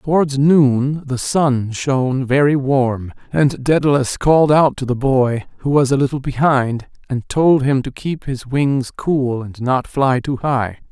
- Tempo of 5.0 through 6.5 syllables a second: No, 4.0 syllables/s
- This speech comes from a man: Yes, male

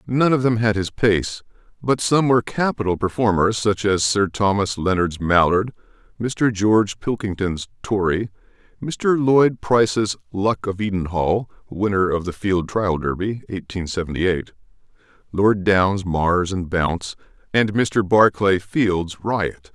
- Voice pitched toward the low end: Yes, low, 100 Hz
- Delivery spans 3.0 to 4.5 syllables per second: Yes, 4.2 syllables/s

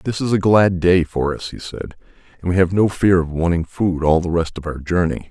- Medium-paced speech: No, fast, 260 wpm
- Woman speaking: No, male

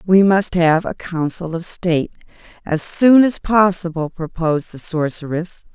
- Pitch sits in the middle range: Yes, medium, 175 Hz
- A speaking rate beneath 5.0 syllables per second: Yes, 4.4 syllables/s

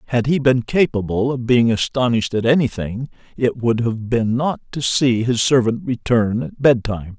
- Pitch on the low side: Yes, low, 120 Hz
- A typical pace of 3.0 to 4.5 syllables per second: No, 4.9 syllables/s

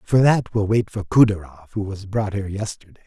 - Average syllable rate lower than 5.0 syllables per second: No, 5.5 syllables/s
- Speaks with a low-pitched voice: Yes, low, 105 Hz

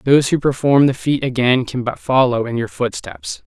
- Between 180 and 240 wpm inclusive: Yes, fast, 205 wpm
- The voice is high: No, low, 130 Hz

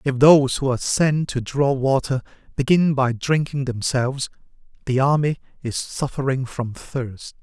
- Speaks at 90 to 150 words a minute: Yes, average, 145 wpm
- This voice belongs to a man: Yes, male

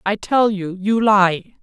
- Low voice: No, high, 200 Hz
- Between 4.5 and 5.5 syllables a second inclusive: No, 3.5 syllables/s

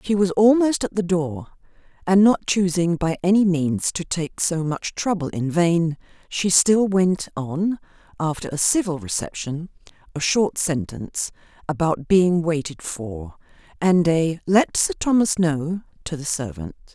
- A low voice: No, medium, 170 Hz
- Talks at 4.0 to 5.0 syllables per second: Yes, 4.1 syllables/s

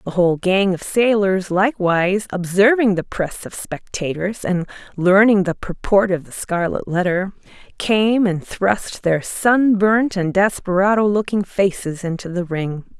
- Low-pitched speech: No, high, 190 Hz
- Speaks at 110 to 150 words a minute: Yes, average, 145 wpm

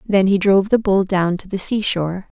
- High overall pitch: Yes, high, 195 Hz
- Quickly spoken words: Yes, fast, 225 wpm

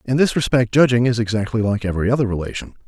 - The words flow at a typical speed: No, fast, 210 wpm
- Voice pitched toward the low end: Yes, low, 115 Hz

